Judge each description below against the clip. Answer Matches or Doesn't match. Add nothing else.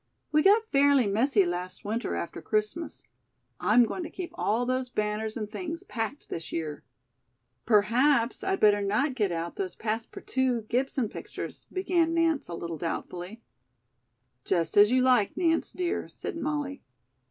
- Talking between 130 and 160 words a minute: Matches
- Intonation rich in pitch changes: Matches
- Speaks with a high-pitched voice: Matches